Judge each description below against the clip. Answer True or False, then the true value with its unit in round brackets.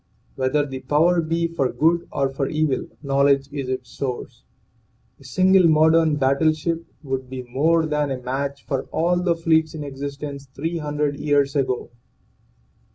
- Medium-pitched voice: True (145 Hz)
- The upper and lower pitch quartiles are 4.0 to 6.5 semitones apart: False (2.8 semitones)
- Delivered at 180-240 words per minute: False (155 wpm)